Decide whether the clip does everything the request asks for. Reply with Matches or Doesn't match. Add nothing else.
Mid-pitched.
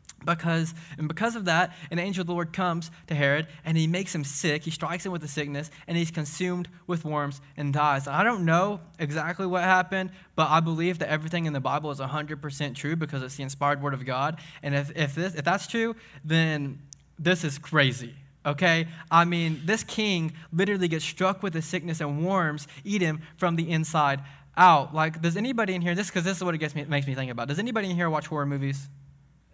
Matches